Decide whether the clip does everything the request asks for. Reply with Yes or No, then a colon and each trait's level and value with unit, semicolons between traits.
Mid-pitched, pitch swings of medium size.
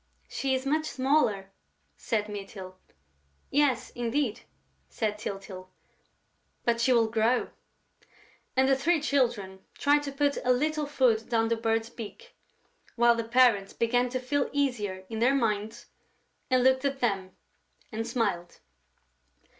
No: high, 240 Hz; average, 3.9 semitones